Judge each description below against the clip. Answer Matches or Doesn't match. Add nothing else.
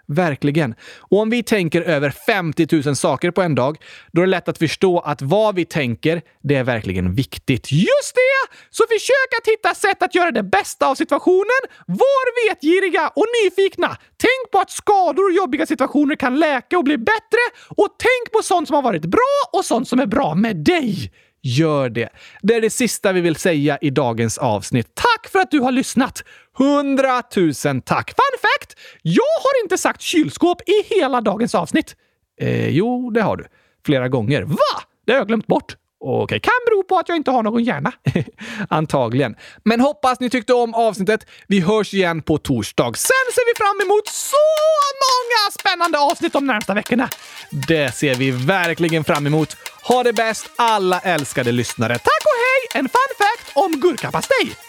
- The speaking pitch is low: Doesn't match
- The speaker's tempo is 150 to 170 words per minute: Doesn't match